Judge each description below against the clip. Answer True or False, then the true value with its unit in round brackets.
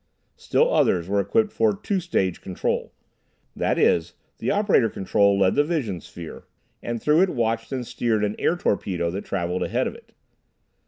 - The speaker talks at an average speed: True (170 wpm)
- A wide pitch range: True (8.5 semitones)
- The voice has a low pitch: True (110 Hz)